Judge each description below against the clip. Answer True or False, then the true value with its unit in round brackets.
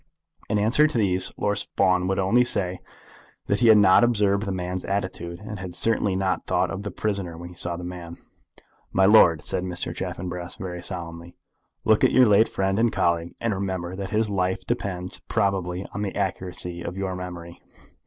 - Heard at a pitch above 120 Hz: False (95 Hz)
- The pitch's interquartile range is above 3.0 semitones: False (2.4 semitones)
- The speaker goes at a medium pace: True (190 wpm)